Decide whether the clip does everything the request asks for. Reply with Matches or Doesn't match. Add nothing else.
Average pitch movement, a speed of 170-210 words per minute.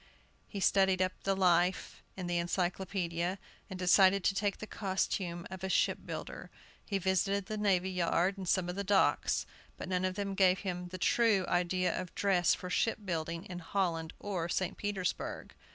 Doesn't match